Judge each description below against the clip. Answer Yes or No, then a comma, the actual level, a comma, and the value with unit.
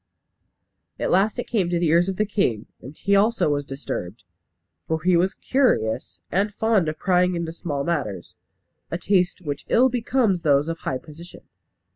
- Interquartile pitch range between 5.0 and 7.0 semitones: Yes, wide, 5.6 semitones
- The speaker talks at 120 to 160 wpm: No, average, 175 wpm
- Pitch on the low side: No, medium, 175 Hz